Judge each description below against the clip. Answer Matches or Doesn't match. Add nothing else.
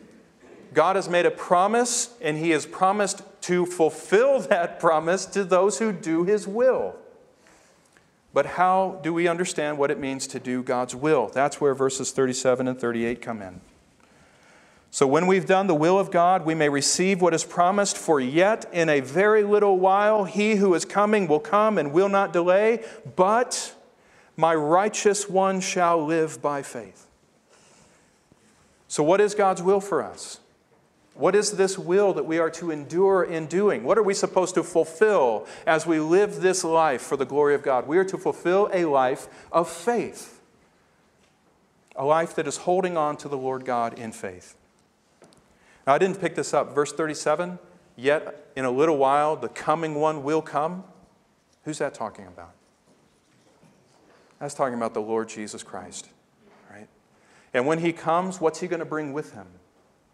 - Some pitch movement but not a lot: Matches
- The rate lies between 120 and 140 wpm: Doesn't match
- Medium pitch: Matches